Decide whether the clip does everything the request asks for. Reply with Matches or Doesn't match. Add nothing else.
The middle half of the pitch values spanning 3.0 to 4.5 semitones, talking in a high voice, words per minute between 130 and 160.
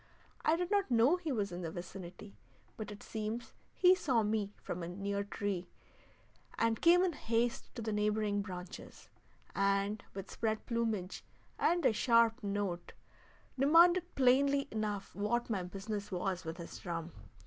Matches